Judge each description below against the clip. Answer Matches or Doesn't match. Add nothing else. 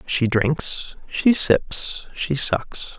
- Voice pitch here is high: Doesn't match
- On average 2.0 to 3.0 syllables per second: Matches